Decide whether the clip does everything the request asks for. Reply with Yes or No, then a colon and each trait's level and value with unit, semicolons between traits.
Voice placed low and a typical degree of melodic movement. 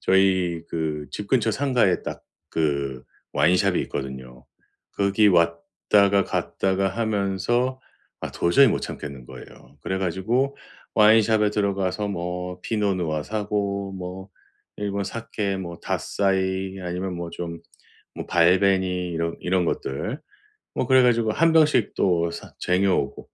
Yes: very low, 95 Hz; average, 3.2 semitones